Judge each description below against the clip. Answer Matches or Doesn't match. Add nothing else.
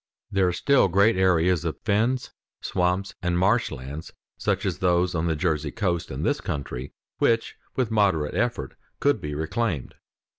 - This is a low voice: Matches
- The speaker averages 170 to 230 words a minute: Doesn't match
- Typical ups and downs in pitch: Matches